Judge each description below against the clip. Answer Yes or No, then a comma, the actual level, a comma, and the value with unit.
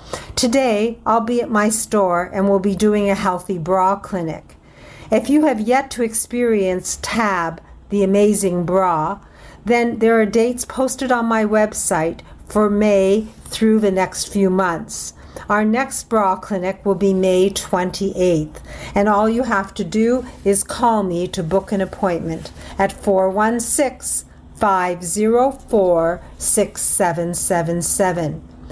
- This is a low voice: No, high, 200 Hz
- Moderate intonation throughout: Yes, average, 3.2 semitones